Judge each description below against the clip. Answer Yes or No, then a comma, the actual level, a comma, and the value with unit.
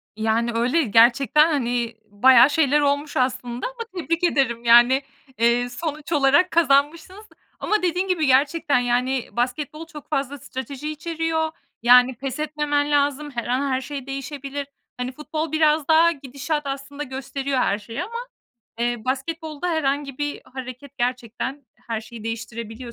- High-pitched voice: Yes, very high, 275 Hz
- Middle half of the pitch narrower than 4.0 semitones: Yes, average, 3.6 semitones